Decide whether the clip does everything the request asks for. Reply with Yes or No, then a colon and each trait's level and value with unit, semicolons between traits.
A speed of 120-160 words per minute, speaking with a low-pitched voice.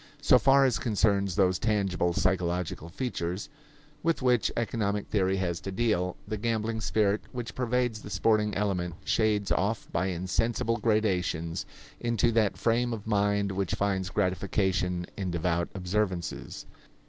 Yes: slow, 135 wpm; low, 100 Hz